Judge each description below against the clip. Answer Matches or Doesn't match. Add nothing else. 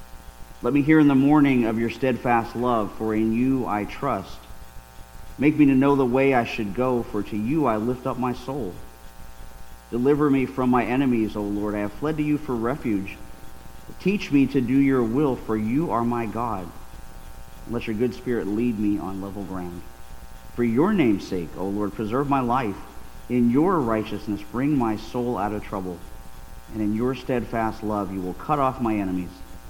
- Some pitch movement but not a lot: Doesn't match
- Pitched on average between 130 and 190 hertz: Doesn't match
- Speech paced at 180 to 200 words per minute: Matches